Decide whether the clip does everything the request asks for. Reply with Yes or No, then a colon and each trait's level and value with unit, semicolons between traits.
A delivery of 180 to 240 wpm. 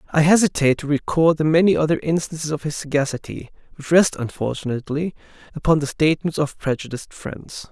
No: average, 155 wpm